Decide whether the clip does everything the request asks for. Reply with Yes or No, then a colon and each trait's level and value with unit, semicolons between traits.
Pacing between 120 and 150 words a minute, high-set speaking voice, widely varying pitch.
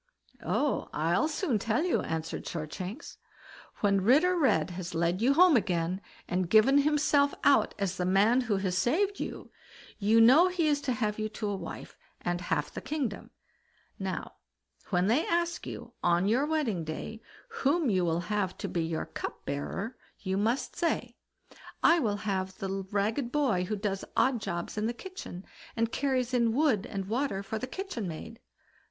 No: average, 170 wpm; high, 215 Hz; wide, 6.8 semitones